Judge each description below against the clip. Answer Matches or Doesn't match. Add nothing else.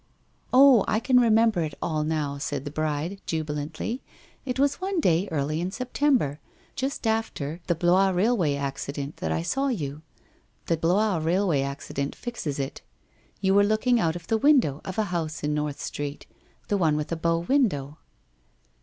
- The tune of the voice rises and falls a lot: Matches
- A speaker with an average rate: Matches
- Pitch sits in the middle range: Matches